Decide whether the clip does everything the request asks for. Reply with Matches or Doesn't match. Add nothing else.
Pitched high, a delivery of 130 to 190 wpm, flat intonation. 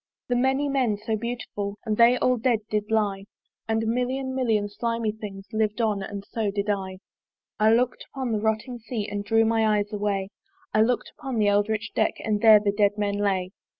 Doesn't match